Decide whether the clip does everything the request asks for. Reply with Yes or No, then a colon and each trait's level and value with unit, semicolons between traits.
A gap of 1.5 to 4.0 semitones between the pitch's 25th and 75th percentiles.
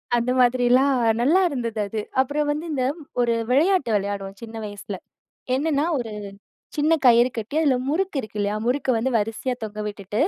No: average, 4.7 semitones